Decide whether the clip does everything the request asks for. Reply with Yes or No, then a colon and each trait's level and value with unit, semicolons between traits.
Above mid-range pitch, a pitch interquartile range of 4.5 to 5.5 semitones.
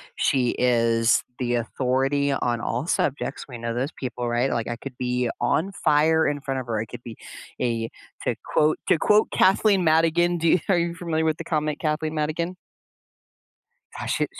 No: medium, 140 Hz; average, 4.8 semitones